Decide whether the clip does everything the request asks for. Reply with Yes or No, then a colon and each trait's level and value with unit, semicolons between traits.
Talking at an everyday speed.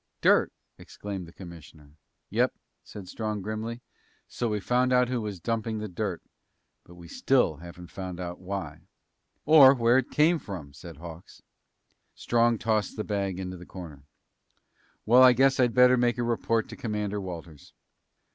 Yes: average, 160 wpm